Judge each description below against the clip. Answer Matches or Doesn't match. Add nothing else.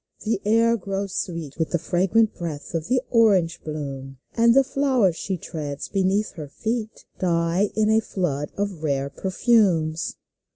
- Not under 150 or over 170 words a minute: Matches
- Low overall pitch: Doesn't match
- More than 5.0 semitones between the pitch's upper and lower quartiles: Matches